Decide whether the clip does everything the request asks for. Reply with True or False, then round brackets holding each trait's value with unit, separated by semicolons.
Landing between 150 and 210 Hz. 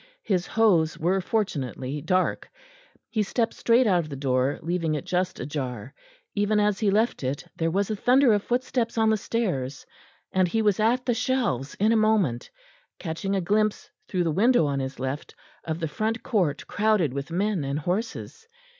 True (190 Hz)